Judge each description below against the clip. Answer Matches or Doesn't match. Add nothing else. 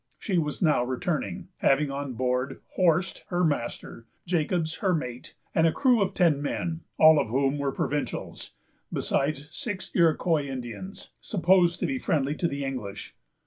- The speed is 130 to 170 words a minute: Matches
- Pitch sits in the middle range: Matches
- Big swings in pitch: Doesn't match